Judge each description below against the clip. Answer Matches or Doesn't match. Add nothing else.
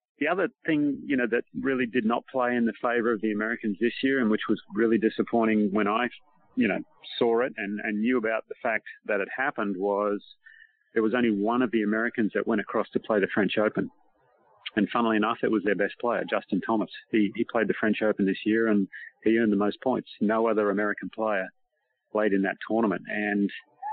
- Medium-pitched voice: Doesn't match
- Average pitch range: Doesn't match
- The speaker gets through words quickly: Matches